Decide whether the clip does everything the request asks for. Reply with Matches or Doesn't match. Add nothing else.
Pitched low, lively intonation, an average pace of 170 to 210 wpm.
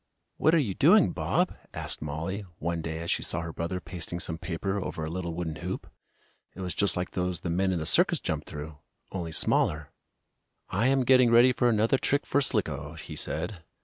Doesn't match